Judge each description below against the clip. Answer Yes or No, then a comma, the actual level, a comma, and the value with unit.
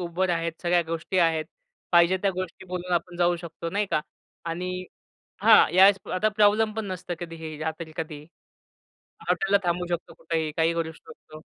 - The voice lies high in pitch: No, medium, 175 Hz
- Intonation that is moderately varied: No, narrow, 2.0 semitones